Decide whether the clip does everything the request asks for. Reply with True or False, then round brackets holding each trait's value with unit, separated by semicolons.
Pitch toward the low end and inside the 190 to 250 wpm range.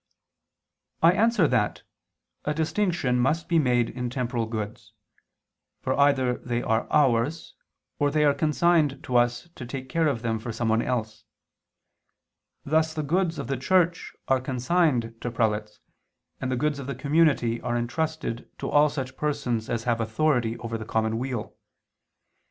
False (130 Hz; 155 wpm)